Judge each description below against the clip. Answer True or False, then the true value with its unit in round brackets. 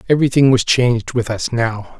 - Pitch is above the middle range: False (120 Hz)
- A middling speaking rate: True (180 wpm)